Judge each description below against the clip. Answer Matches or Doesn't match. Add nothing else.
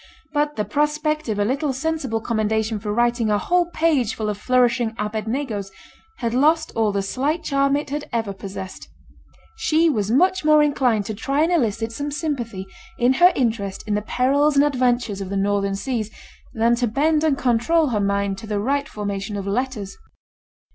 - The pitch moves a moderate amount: Doesn't match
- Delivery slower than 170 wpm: Doesn't match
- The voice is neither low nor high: Doesn't match